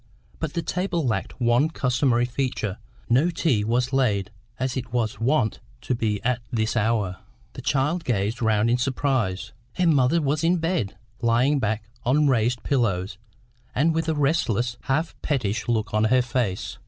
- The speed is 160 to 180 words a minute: Yes, average, 165 wpm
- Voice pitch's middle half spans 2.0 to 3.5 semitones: No, average, 4.5 semitones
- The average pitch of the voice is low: Yes, low, 125 Hz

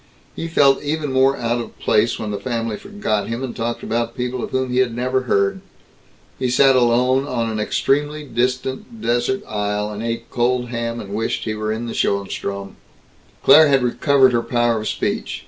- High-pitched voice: No, low, 120 Hz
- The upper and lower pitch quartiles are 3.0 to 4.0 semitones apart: No, narrow, 2.6 semitones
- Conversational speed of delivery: Yes, average, 185 wpm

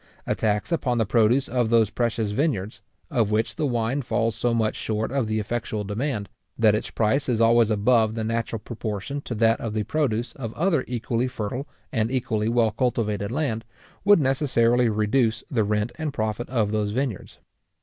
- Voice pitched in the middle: No, low, 115 Hz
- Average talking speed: Yes, average, 180 wpm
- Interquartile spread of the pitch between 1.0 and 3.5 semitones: Yes, narrow, 2.6 semitones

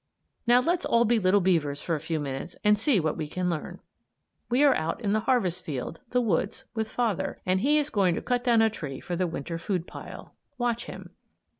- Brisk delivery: Yes, fast, 215 wpm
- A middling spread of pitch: No, wide, 6.2 semitones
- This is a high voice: Yes, high, 195 Hz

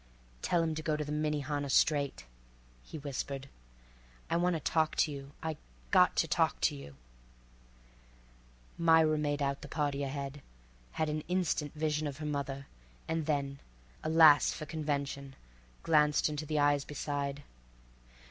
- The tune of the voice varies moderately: No, narrow, 1.8 semitones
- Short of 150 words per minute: Yes, slow, 135 wpm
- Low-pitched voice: No, medium, 145 Hz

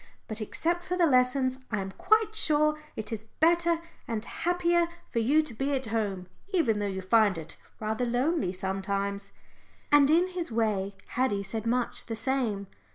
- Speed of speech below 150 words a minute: No, average, 170 wpm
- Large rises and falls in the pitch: Yes, wide, 7.1 semitones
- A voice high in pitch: Yes, high, 235 Hz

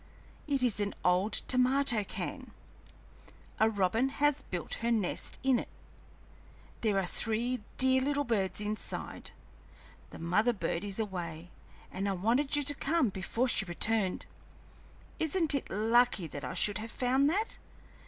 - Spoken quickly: No, average, 145 wpm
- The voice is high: Yes, high, 225 Hz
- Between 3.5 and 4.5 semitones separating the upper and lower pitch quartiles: No, average, 5.3 semitones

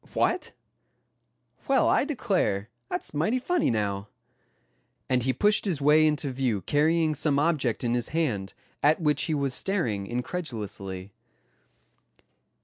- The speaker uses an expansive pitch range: Yes, wide, 6.3 semitones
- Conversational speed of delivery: No, slow, 130 wpm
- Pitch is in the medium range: Yes, medium, 145 Hz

